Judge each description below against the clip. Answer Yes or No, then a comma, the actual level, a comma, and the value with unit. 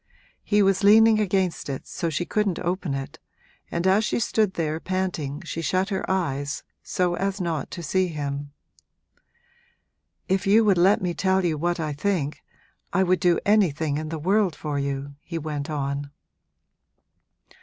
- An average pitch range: Yes, average, 4.3 semitones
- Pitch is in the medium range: Yes, medium, 175 Hz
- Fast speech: No, average, 165 wpm